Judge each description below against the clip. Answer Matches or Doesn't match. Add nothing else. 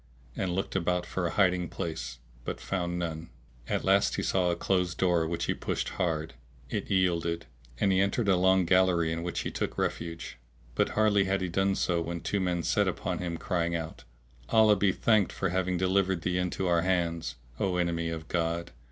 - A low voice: Matches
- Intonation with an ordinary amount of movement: Doesn't match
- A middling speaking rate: Matches